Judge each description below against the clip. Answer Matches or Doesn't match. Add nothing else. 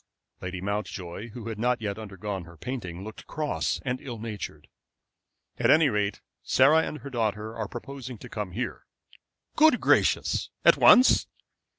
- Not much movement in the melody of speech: Doesn't match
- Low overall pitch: Matches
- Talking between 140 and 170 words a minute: Matches